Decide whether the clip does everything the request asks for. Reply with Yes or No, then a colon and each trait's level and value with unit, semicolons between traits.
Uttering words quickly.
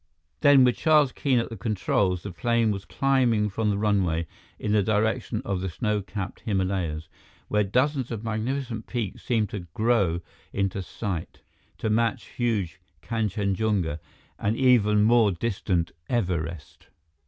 No: average, 140 wpm